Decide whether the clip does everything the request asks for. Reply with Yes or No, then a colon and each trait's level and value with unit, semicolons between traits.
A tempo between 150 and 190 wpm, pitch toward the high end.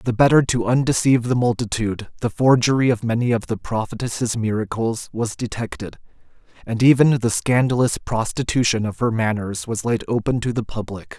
No: average, 160 wpm; low, 115 Hz